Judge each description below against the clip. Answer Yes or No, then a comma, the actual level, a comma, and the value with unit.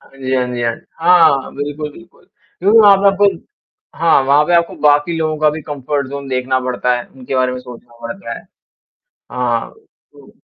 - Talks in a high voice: No, medium, 140 Hz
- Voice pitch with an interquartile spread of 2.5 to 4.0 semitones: No, average, 4.5 semitones